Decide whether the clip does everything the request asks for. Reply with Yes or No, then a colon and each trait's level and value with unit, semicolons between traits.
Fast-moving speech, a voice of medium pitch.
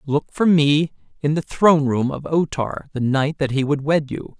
Yes: fast, 230 wpm; medium, 145 Hz